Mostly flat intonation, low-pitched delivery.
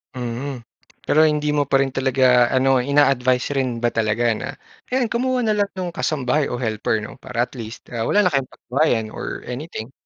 No: average, 3.7 semitones; low, 130 Hz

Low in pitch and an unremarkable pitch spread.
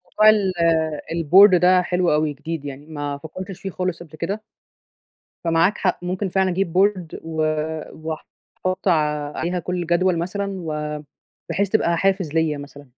No: medium, 175 Hz; average, 3.1 semitones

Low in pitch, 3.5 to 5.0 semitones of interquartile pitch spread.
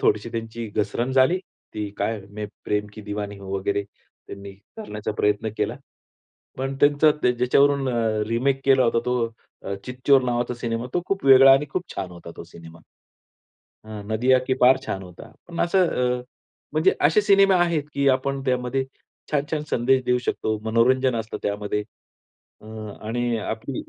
Yes: low, 125 Hz; average, 4.1 semitones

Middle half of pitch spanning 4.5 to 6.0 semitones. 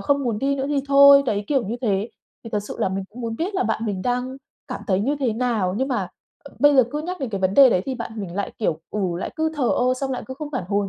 Yes: average, 5.2 semitones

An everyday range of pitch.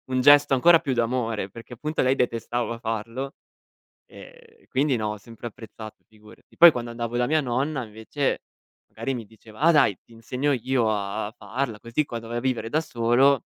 Yes: average, 3.4 semitones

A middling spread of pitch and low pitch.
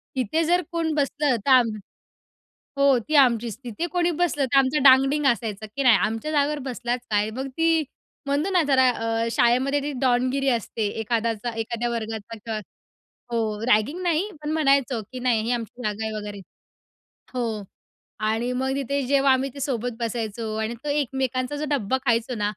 No: average, 3.7 semitones; very high, 250 Hz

